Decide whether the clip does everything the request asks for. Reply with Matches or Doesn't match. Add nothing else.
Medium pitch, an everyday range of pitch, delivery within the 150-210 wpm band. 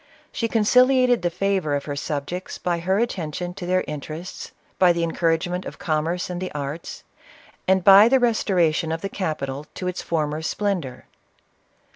Matches